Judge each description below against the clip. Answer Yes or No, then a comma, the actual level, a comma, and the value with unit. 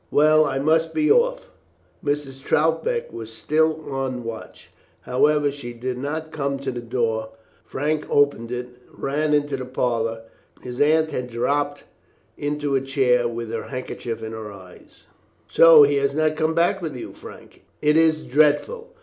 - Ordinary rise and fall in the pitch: Yes, average, 3.9 semitones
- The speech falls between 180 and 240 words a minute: No, average, 165 wpm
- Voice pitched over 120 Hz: Yes, medium, 140 Hz